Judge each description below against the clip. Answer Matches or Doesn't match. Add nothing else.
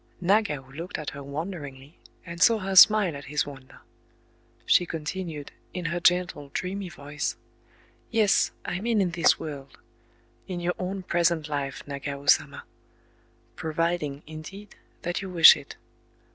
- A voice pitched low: Doesn't match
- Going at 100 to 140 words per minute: Matches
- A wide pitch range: Doesn't match